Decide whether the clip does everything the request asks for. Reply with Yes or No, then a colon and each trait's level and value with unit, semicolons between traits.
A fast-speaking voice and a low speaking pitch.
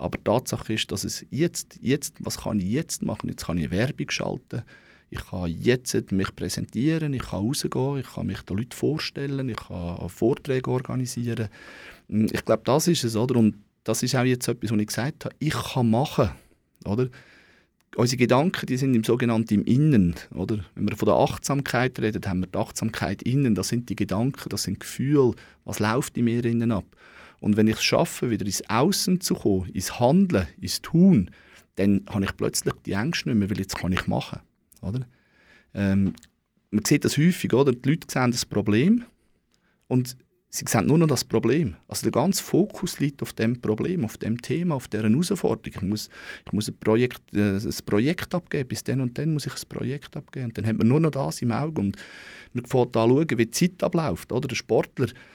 Yes: fast, 205 wpm; low, 120 Hz